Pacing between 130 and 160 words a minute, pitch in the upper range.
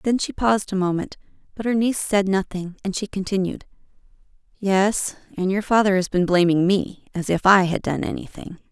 No: average, 170 wpm; high, 195 Hz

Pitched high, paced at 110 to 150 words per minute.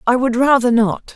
No: high, 245 Hz; fast, 210 wpm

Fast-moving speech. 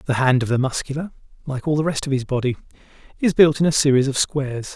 Yes: fast, 240 wpm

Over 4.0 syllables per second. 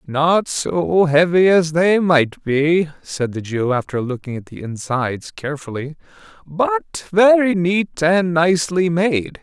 No: 3.8 syllables/s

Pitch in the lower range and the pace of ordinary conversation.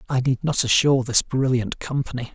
Yes: low, 130 Hz; average, 180 wpm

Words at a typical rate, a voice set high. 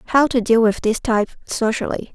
Yes: average, 195 wpm; high, 230 Hz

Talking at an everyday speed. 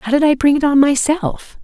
No: fast, 255 wpm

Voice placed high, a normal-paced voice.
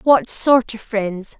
Yes: high, 225 Hz; average, 170 wpm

